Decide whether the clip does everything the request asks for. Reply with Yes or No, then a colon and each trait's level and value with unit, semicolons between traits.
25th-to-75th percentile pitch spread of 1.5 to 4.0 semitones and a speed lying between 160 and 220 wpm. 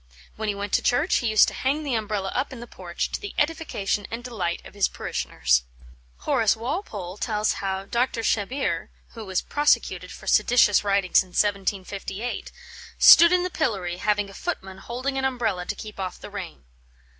No: average, 4.5 semitones; average, 180 wpm